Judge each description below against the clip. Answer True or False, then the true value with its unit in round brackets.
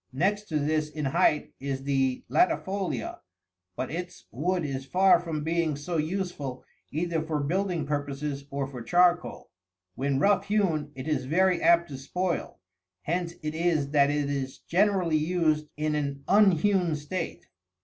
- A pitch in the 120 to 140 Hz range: False (155 Hz)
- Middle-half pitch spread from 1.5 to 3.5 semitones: False (4.0 semitones)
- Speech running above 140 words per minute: True (150 wpm)